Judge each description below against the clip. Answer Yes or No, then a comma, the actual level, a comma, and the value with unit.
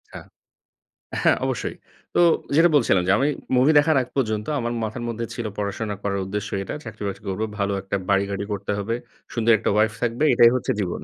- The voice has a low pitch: Yes, low, 110 Hz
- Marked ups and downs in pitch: No, average, 2.8 semitones